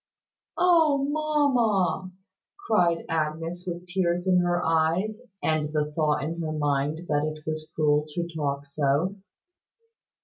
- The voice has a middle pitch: Yes, medium, 165 Hz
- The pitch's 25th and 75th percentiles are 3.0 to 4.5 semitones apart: Yes, average, 3.5 semitones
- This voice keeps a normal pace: No, slow, 130 wpm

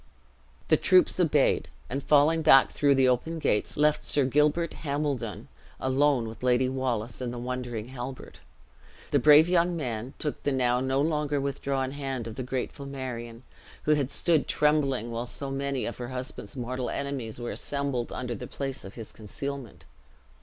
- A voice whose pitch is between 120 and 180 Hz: Yes, low, 135 Hz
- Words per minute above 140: Yes, average, 165 wpm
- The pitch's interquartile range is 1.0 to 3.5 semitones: Yes, average, 2.8 semitones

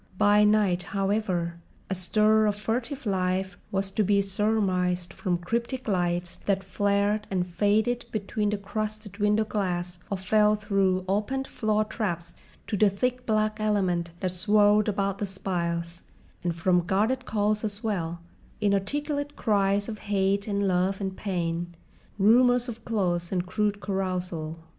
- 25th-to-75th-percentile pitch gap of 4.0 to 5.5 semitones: No, average, 2.7 semitones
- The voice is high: Yes, high, 200 Hz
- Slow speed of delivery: No, average, 145 wpm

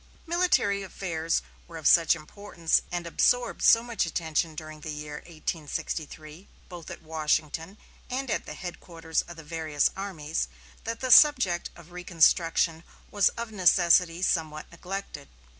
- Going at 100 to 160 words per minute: Yes, average, 140 wpm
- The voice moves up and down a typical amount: Yes, average, 3.6 semitones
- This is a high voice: No, medium, 170 Hz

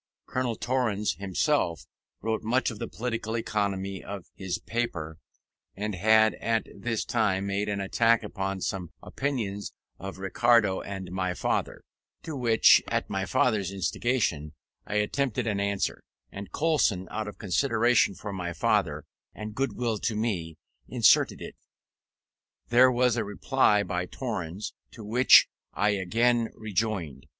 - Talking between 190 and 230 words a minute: No, average, 140 wpm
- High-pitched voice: No, low, 105 Hz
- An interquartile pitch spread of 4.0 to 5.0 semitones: No, average, 3.5 semitones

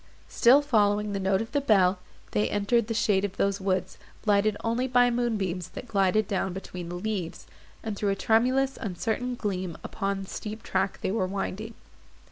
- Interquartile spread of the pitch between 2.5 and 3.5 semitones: Yes, average, 3.0 semitones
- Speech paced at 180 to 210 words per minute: Yes, average, 185 wpm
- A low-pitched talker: No, high, 205 Hz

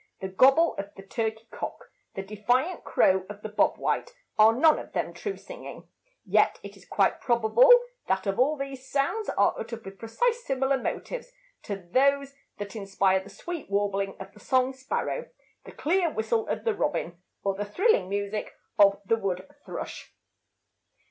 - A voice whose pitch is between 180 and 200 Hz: No, high, 225 Hz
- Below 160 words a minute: No, average, 170 wpm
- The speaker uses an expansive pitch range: Yes, wide, 6.0 semitones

